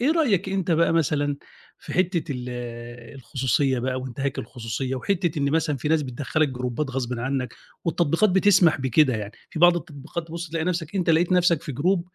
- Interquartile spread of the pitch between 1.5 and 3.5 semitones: No, average, 4.7 semitones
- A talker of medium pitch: Yes, medium, 150 Hz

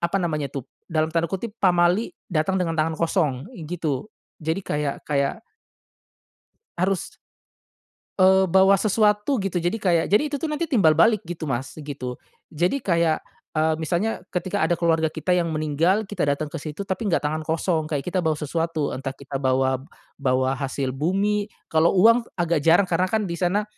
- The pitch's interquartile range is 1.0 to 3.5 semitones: No, average, 4.1 semitones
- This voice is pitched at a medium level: Yes, medium, 170 Hz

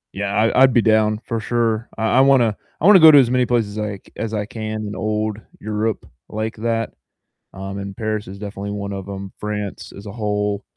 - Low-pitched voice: Yes, low, 110 Hz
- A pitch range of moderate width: No, narrow, 1.9 semitones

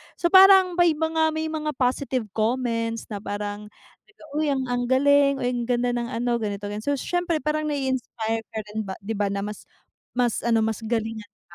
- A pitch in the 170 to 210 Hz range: No, high, 245 Hz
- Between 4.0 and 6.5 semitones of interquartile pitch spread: Yes, average, 5.3 semitones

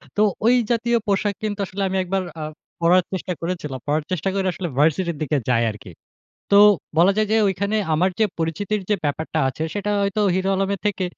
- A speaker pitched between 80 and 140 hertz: No, medium, 185 Hz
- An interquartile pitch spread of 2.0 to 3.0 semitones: No, average, 3.9 semitones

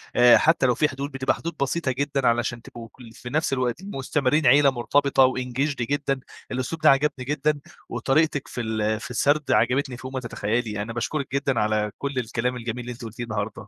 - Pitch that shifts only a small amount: No, average, 3.0 semitones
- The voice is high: No, low, 130 Hz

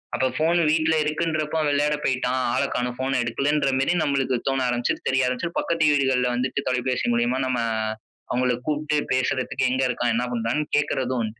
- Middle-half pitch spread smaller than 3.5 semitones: Yes, average, 3.1 semitones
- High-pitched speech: No, low, 130 Hz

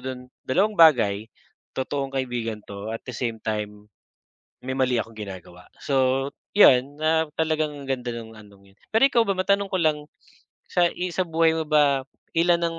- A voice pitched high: No, low, 135 Hz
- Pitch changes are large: Yes, wide, 6.2 semitones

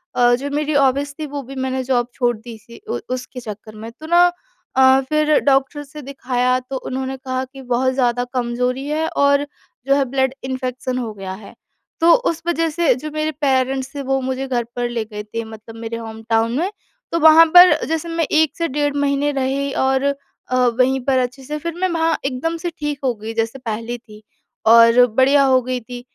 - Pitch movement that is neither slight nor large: Yes, average, 3.0 semitones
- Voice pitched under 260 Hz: No, very high, 265 Hz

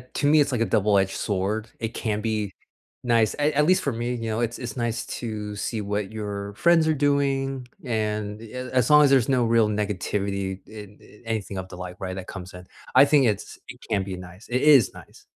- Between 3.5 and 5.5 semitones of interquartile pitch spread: Yes, average, 3.9 semitones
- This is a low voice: Yes, low, 110 Hz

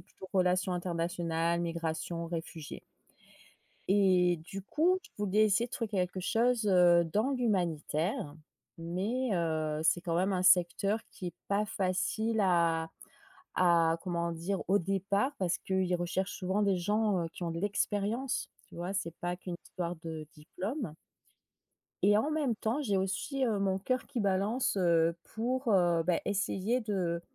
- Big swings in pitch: No, average, 3.4 semitones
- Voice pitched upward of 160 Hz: Yes, medium, 185 Hz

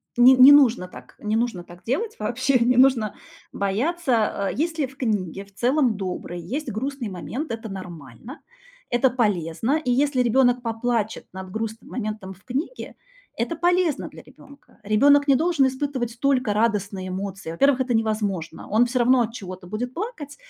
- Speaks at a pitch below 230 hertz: No, high, 235 Hz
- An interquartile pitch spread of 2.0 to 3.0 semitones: No, average, 5.0 semitones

